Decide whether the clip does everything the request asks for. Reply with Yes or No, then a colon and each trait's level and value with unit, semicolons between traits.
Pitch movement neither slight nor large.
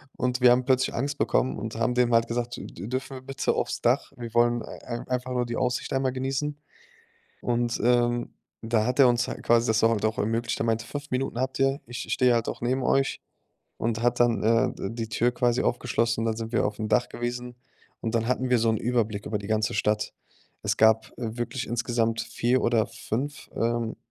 No: narrow, 1.8 semitones